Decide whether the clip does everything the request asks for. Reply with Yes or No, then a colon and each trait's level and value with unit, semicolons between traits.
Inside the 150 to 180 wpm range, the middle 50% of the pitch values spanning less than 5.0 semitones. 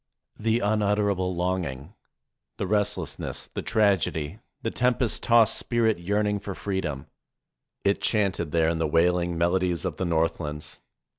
No: average, 140 wpm; average, 3.8 semitones